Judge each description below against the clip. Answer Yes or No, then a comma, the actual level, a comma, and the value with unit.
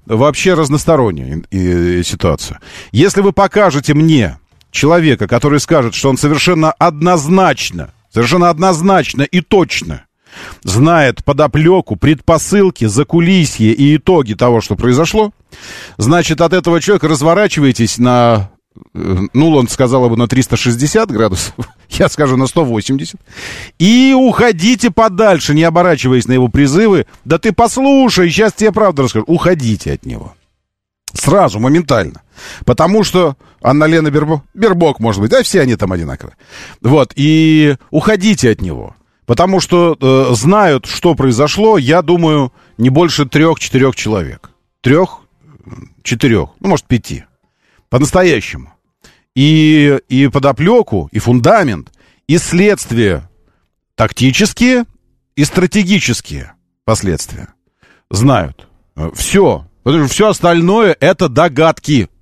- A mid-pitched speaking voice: Yes, medium, 150 Hz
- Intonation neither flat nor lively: No, wide, 7.2 semitones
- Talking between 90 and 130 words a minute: Yes, average, 115 wpm